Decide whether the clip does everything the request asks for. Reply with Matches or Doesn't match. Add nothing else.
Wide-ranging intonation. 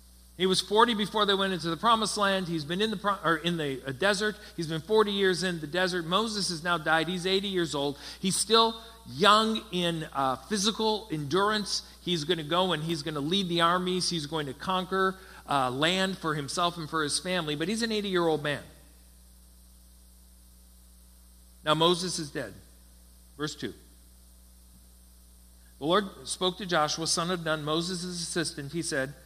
Matches